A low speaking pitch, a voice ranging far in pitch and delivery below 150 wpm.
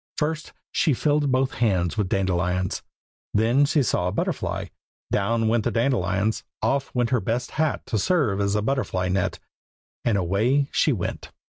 No: low, 115 Hz; wide, 5.8 semitones; average, 160 wpm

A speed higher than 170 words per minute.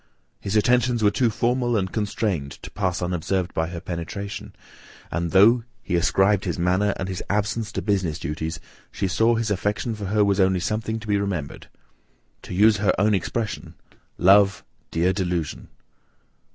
No: average, 165 wpm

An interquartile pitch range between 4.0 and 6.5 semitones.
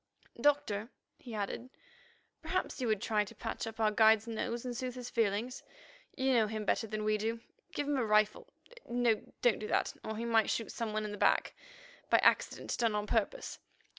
No: narrow, 2.4 semitones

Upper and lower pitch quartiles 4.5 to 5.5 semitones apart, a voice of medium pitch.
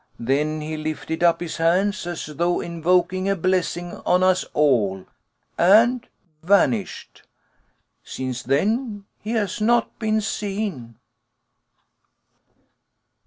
Yes: average, 4.8 semitones; medium, 175 Hz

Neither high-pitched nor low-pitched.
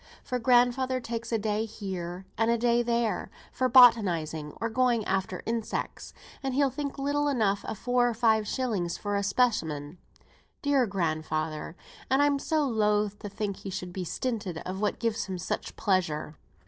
No: high, 220 Hz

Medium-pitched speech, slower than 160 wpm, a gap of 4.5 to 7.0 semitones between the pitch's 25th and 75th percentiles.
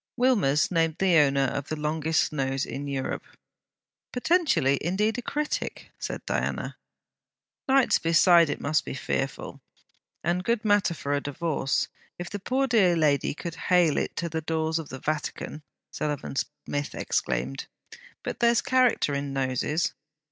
Yes: medium, 160 Hz; average, 150 wpm; wide, 5.4 semitones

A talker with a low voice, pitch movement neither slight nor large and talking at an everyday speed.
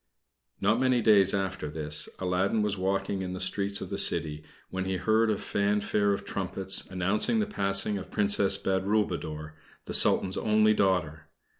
No: low, 100 Hz; narrow, 2.1 semitones; average, 165 wpm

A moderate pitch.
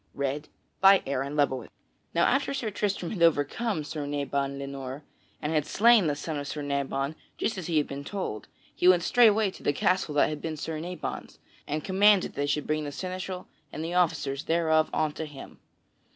Yes: medium, 155 Hz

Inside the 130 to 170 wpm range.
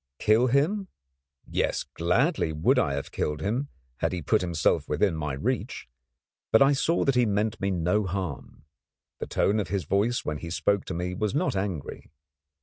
No: average, 180 wpm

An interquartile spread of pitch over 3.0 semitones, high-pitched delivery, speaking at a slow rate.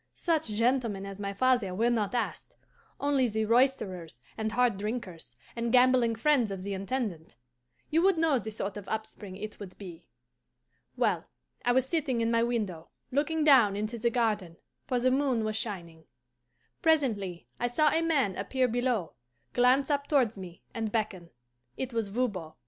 No: average, 4.5 semitones; high, 230 Hz; average, 165 wpm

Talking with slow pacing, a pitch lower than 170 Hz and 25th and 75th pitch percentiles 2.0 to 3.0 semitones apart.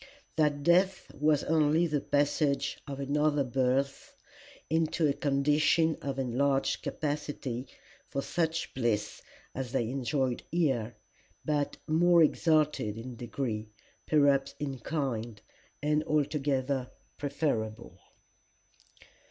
Yes: slow, 105 wpm; medium, 140 Hz; average, 2.7 semitones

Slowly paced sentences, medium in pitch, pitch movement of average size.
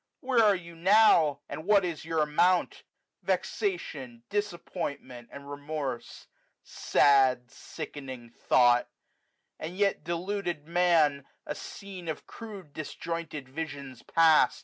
Yes: slow, 120 wpm; medium, 160 Hz; average, 4.3 semitones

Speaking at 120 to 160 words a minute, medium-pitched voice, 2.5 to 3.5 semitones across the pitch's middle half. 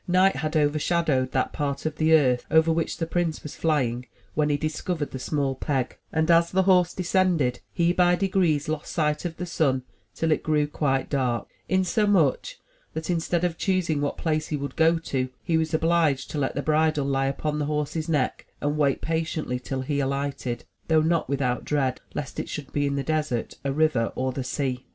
No: average, 200 wpm; medium, 150 Hz; average, 3.1 semitones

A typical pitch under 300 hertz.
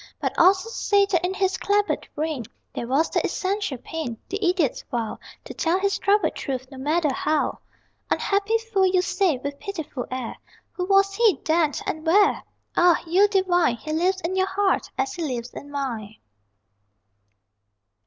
No: very high, 350 Hz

